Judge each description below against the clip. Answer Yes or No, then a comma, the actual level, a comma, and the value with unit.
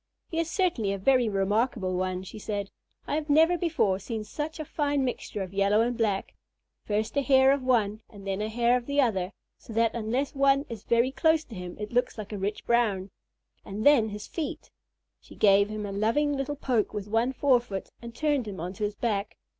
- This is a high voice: Yes, high, 225 Hz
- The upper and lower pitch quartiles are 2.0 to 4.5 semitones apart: No, average, 5.0 semitones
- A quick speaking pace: Yes, fast, 210 wpm